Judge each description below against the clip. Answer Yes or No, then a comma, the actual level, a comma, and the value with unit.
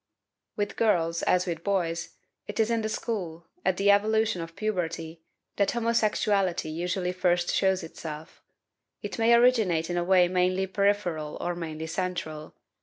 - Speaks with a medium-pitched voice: Yes, medium, 180 Hz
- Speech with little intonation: No, average, 3.6 semitones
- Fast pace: No, average, 150 wpm